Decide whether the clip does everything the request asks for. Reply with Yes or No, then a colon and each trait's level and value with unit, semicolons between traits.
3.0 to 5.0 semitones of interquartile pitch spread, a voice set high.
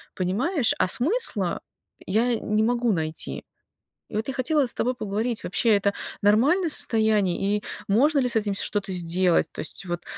Yes: average, 4.3 semitones; high, 220 Hz